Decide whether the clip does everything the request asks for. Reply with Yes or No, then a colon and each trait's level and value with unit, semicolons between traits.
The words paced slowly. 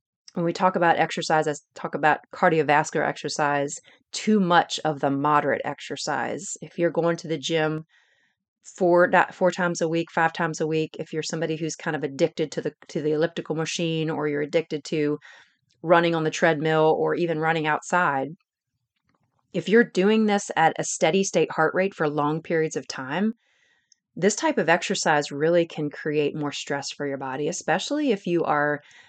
No: average, 180 wpm